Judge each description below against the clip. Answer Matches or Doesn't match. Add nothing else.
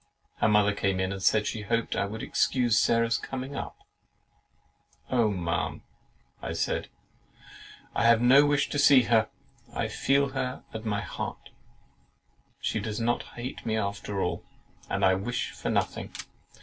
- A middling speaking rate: Matches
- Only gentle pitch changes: Doesn't match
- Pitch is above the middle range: Doesn't match